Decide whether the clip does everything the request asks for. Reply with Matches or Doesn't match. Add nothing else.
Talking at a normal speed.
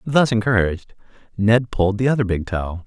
Matches